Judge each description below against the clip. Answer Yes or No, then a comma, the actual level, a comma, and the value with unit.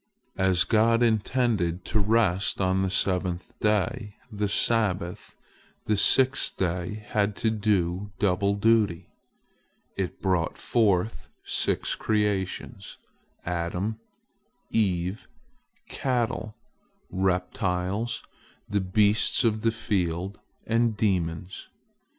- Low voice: Yes, low, 100 Hz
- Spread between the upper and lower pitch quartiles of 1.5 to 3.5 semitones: Yes, average, 3.1 semitones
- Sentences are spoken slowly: Yes, slow, 95 wpm